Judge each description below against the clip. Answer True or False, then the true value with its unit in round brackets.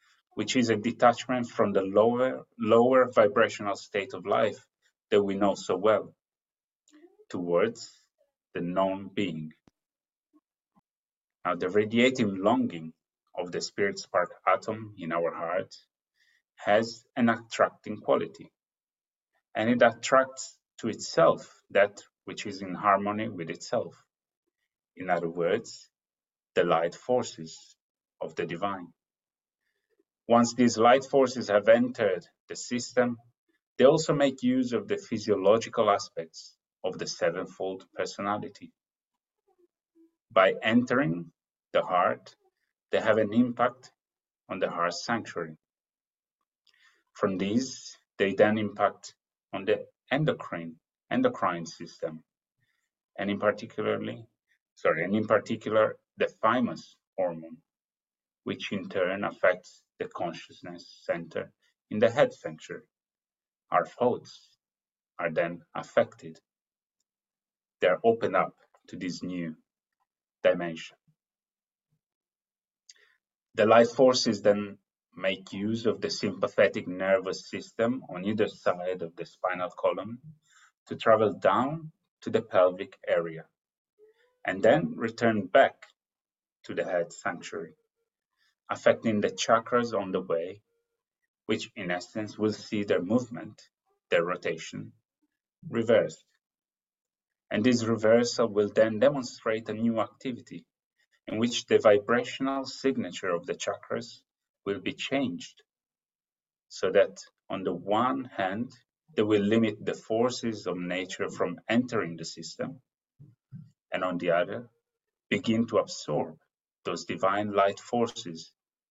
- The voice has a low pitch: True (115 Hz)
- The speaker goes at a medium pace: False (115 wpm)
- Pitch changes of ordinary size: False (7.1 semitones)